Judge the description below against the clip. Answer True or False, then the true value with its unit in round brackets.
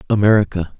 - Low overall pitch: True (95 Hz)